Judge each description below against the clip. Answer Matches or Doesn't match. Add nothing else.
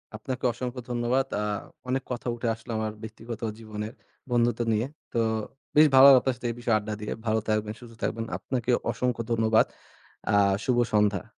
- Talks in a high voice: Doesn't match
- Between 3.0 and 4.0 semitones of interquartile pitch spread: Doesn't match